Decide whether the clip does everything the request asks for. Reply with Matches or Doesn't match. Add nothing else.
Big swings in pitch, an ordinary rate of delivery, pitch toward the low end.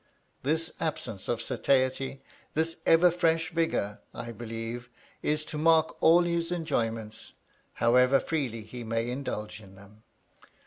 Doesn't match